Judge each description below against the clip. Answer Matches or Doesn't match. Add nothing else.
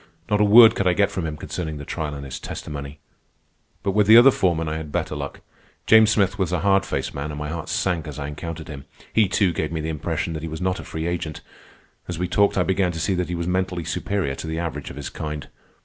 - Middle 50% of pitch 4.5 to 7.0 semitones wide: Doesn't match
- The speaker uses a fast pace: Matches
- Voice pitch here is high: Doesn't match